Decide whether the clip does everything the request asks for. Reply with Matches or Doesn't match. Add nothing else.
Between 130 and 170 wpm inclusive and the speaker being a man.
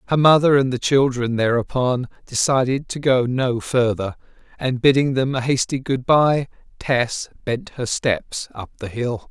Matches